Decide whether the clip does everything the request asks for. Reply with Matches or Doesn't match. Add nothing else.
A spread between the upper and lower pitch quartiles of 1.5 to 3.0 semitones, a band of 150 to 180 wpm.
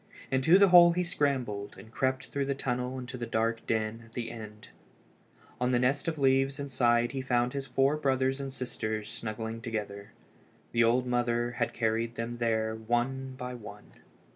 Matches